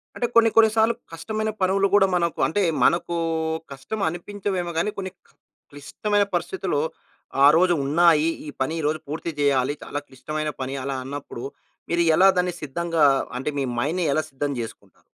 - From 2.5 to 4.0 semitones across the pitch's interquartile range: No, average, 4.8 semitones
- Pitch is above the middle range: No, medium, 170 Hz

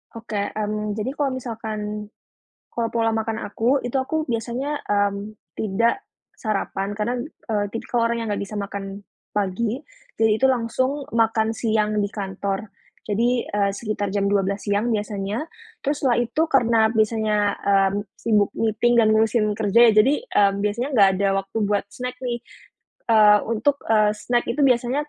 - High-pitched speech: Yes, high, 220 Hz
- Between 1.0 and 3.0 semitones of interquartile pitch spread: Yes, narrow, 2.5 semitones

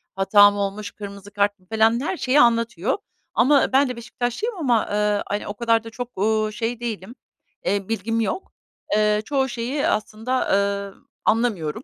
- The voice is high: Yes, high, 220 Hz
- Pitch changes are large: No, average, 3.1 semitones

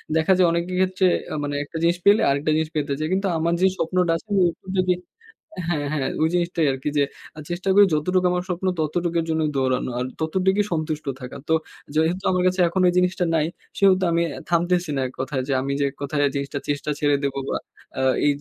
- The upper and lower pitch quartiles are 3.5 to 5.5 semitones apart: Yes, average, 3.8 semitones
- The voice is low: No, medium, 165 Hz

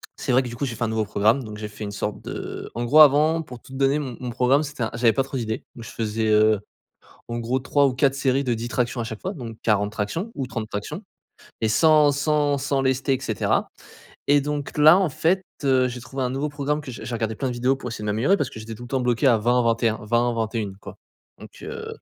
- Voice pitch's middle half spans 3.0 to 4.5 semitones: Yes, average, 3.6 semitones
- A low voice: Yes, low, 125 Hz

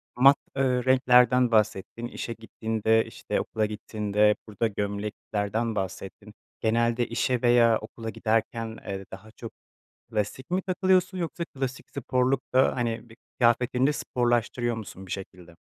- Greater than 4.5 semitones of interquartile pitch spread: No, average, 2.8 semitones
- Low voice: Yes, low, 115 Hz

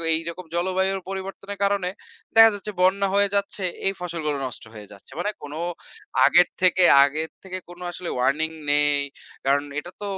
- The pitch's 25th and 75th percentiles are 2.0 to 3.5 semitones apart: No, average, 4.2 semitones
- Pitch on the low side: No, medium, 180 Hz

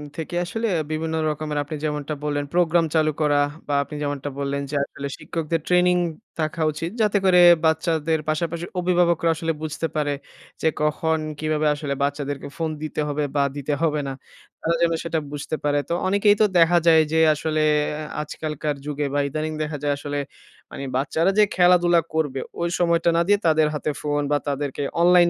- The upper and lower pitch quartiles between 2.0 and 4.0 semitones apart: Yes, narrow, 2.4 semitones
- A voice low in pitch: No, medium, 155 Hz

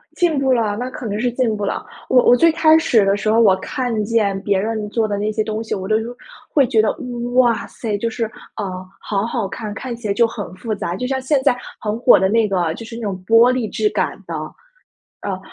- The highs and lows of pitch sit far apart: No, average, 3.1 semitones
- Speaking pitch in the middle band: No, high, 225 Hz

